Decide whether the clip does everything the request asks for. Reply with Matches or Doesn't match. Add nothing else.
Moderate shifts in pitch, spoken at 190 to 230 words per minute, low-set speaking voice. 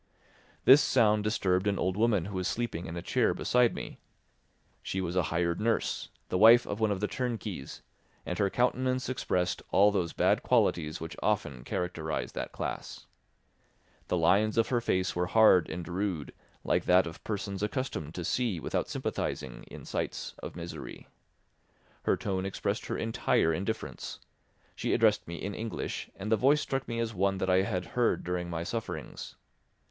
Doesn't match